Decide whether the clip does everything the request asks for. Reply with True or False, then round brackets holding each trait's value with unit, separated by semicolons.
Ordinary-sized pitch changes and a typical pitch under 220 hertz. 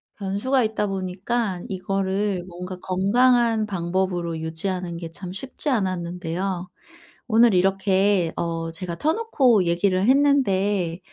True (3.2 semitones; 190 Hz)